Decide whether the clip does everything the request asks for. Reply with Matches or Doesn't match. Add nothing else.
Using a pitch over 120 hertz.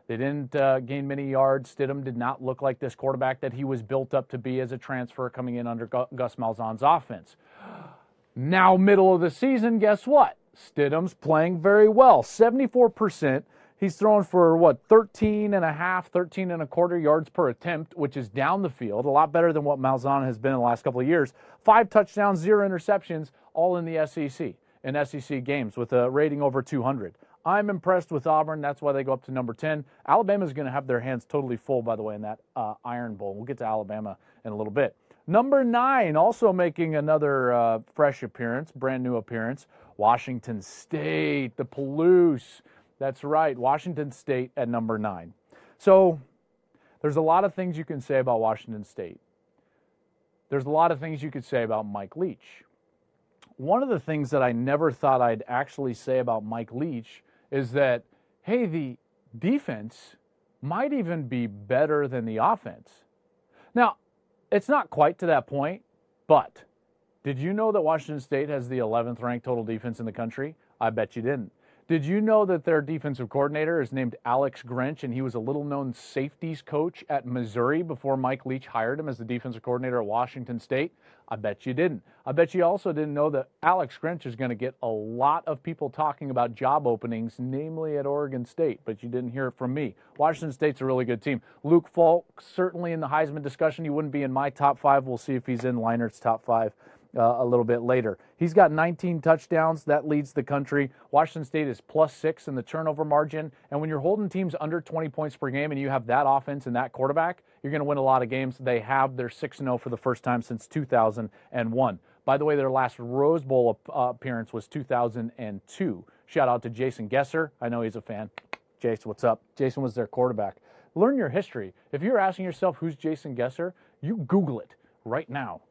Matches